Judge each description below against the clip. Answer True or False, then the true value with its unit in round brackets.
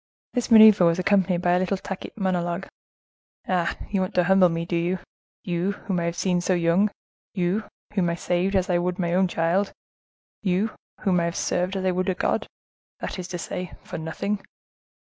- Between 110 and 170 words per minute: False (185 wpm)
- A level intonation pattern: True (1.8 semitones)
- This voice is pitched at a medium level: True (180 Hz)